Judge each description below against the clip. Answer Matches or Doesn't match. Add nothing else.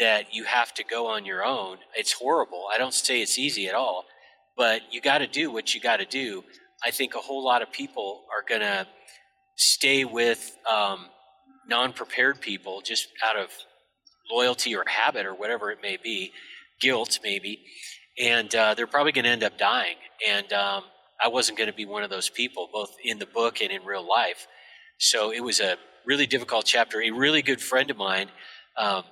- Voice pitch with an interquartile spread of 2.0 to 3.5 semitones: Doesn't match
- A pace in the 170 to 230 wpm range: Matches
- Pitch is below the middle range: Matches